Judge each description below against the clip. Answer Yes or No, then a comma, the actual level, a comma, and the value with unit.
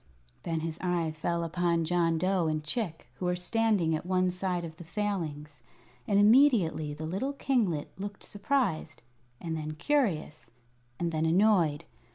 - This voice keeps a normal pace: Yes, average, 155 wpm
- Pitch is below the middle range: No, medium, 175 Hz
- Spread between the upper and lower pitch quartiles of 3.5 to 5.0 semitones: Yes, average, 4.0 semitones